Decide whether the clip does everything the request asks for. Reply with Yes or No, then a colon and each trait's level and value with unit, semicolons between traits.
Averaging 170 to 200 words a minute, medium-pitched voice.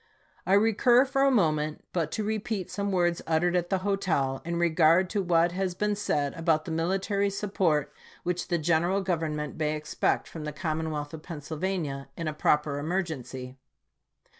Yes: average, 175 wpm; medium, 170 Hz